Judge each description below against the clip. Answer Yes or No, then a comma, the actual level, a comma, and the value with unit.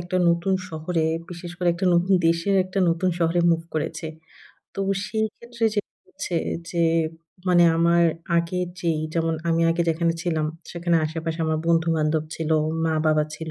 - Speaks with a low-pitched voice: No, medium, 170 Hz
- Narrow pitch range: Yes, narrow, 1.4 semitones